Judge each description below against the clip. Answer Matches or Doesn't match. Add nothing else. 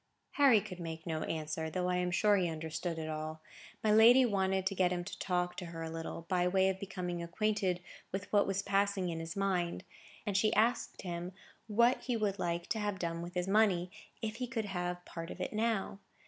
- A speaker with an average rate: Doesn't match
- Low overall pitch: Doesn't match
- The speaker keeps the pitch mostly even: Doesn't match